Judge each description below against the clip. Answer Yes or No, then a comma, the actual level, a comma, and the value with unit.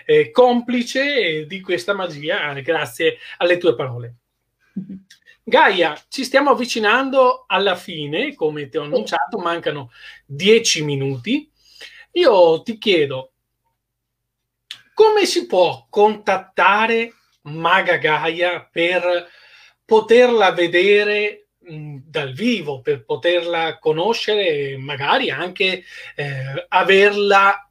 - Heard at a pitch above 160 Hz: Yes, medium, 185 Hz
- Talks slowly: Yes, slow, 95 wpm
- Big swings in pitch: Yes, wide, 7.7 semitones